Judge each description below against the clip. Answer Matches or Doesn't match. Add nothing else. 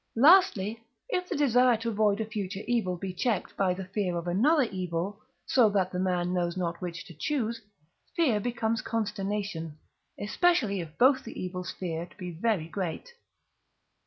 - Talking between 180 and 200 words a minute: Doesn't match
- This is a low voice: Doesn't match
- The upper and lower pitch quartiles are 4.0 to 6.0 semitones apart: Matches